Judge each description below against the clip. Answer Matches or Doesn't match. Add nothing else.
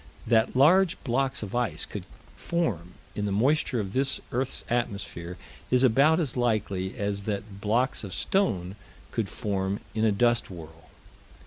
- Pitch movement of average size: Matches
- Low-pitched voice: Matches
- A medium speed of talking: Matches